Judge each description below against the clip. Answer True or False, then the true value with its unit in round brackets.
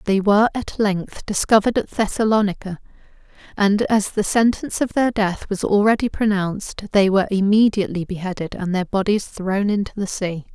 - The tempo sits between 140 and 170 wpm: True (160 wpm)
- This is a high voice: True (200 Hz)